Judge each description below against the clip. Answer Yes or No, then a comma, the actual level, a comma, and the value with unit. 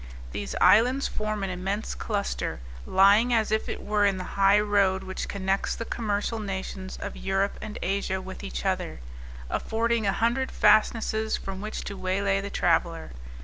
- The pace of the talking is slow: No, average, 165 wpm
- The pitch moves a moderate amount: No, narrow, 2.3 semitones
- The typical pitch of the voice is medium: No, high, 200 Hz